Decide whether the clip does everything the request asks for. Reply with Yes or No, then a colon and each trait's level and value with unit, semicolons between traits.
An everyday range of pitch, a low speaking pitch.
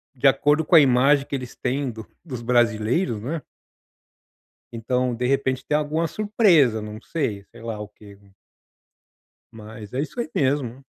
Yes: average, 4.5 semitones; low, 125 Hz